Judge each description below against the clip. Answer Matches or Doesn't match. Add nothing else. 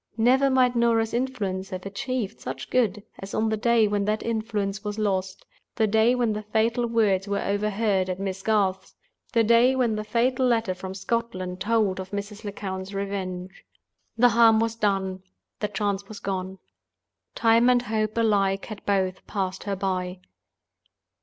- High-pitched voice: Matches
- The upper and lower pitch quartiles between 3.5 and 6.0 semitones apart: Doesn't match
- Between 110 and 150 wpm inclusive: Doesn't match